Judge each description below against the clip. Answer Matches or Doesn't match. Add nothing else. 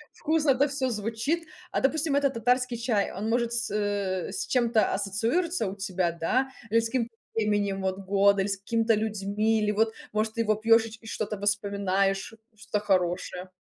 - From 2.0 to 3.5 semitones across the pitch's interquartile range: Matches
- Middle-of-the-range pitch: Doesn't match